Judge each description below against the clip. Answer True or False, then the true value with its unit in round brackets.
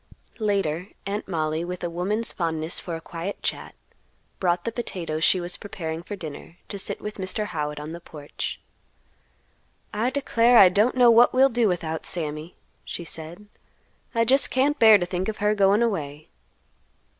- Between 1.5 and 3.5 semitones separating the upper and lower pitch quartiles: False (4.8 semitones)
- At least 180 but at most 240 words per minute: False (170 wpm)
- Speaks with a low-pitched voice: False (185 Hz)